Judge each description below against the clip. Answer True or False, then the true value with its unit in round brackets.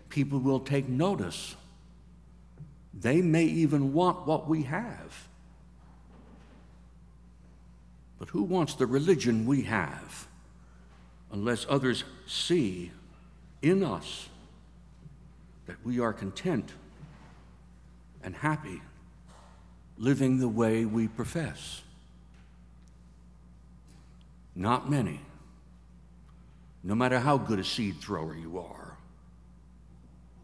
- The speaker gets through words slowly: True (90 wpm)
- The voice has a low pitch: True (80 Hz)